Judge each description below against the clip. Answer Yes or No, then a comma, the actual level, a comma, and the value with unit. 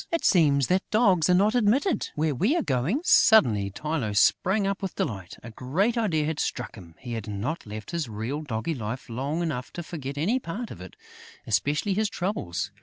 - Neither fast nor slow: Yes, average, 195 wpm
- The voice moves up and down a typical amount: No, wide, 9.0 semitones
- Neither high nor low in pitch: Yes, medium, 150 Hz